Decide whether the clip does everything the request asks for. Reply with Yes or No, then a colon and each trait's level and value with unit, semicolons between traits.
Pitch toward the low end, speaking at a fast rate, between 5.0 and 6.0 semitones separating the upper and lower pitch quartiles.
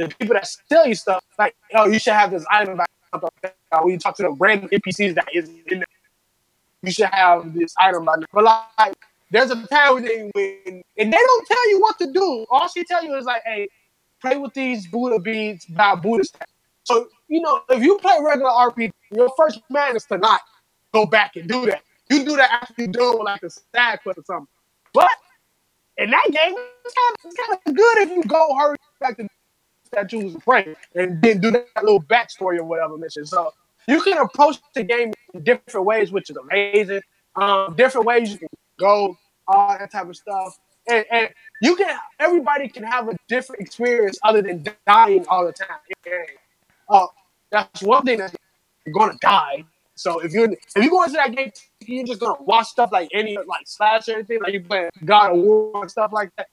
No: high, 220 Hz; fast, 215 wpm; average, 5.3 semitones